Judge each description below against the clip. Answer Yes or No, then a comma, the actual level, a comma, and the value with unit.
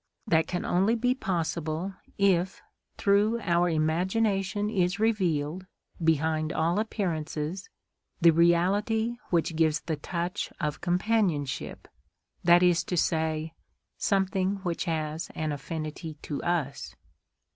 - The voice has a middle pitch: Yes, medium, 175 Hz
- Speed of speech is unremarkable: No, slow, 115 wpm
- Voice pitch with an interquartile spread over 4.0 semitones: No, average, 3.6 semitones